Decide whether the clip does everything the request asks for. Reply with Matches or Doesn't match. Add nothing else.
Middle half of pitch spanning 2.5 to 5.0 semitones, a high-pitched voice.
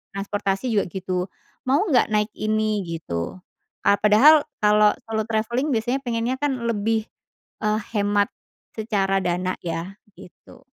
Matches